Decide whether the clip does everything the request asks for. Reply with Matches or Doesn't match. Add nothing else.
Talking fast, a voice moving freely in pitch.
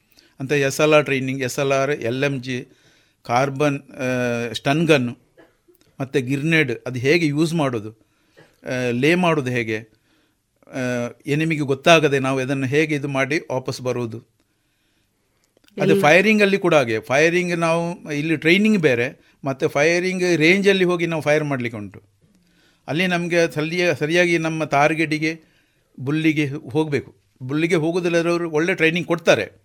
Doesn't match